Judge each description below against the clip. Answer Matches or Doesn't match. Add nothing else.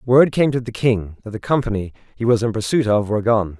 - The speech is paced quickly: Matches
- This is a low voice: Matches